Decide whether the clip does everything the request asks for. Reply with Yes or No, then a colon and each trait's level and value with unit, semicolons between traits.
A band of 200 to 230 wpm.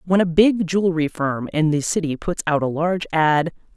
Yes: fast, 205 wpm